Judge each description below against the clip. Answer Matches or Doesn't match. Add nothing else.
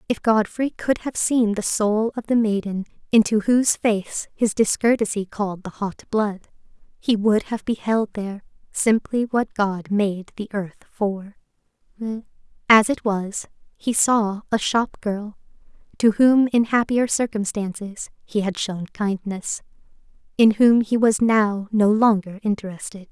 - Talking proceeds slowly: Doesn't match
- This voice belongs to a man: Doesn't match